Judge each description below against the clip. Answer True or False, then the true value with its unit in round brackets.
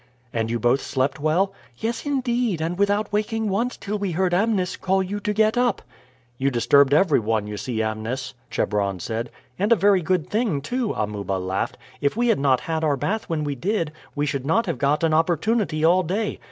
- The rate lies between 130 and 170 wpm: False (200 wpm)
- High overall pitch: False (165 Hz)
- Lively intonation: True (7.8 semitones)